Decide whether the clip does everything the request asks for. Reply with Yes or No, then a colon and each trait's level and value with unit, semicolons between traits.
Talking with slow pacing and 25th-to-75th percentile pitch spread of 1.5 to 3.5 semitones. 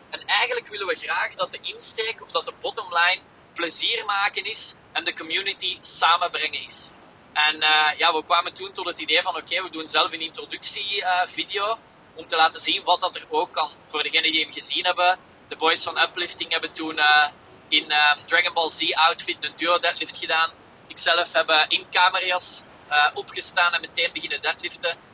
No: average, 195 wpm; average, 3.2 semitones